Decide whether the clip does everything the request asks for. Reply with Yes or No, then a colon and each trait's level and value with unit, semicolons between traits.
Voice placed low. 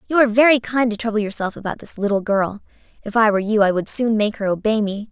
No: high, 215 Hz